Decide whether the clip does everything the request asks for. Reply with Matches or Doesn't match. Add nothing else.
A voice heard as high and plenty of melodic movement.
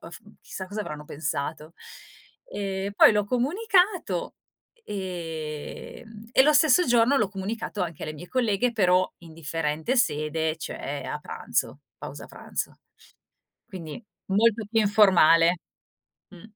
Matches